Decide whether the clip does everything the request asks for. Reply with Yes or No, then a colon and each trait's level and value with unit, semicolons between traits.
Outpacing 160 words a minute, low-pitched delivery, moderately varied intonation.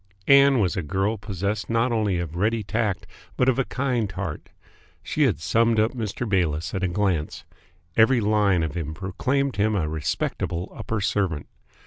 Yes: average, 170 wpm; low, 100 Hz; average, 4.5 semitones